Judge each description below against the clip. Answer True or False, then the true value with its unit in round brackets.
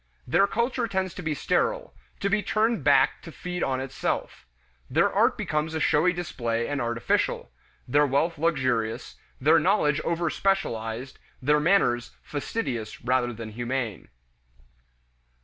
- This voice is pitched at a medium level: True (150 Hz)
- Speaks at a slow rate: True (130 wpm)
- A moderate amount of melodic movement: False (6.7 semitones)